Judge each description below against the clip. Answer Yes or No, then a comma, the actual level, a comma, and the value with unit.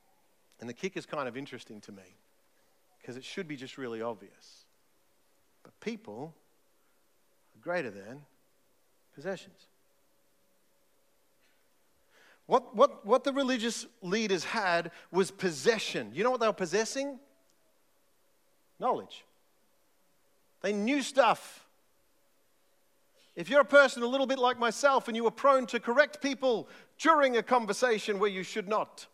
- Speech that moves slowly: Yes, slow, 130 wpm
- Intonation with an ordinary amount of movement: No, wide, 7.2 semitones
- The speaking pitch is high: Yes, high, 215 Hz